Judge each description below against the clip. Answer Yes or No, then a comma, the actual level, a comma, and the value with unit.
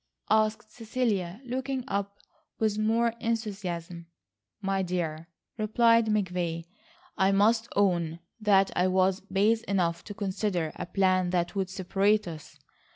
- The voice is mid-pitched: No, high, 195 Hz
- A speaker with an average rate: No, slow, 125 wpm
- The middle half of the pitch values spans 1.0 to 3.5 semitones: Yes, average, 3.2 semitones